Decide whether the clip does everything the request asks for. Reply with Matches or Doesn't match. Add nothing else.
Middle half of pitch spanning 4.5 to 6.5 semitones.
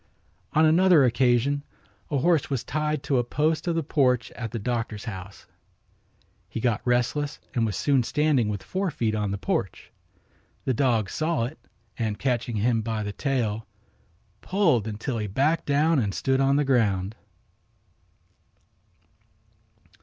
Matches